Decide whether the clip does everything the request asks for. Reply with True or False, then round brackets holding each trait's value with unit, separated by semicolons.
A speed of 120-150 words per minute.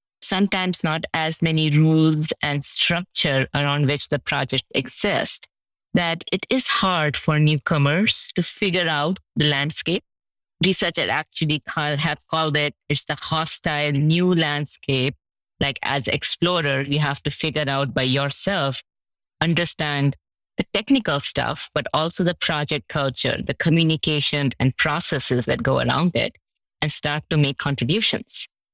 True (140 wpm)